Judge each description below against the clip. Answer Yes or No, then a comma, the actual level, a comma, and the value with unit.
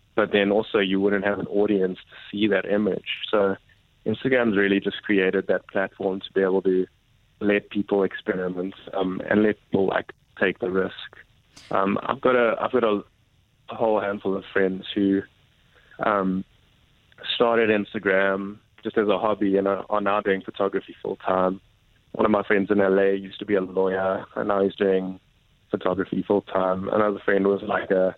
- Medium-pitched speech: No, low, 100 Hz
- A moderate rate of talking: Yes, average, 175 wpm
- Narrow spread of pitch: Yes, narrow, 1.6 semitones